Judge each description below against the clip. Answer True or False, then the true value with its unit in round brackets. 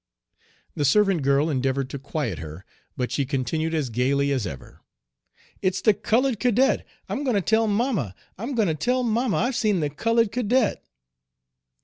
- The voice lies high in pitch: False (180 Hz)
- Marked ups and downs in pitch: True (8.8 semitones)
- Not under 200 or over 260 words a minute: False (165 wpm)